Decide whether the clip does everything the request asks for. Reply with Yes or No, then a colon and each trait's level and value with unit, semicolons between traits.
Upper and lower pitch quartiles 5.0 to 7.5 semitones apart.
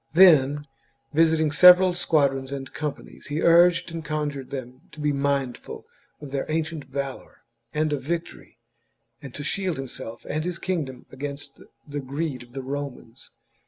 No: average, 3.2 semitones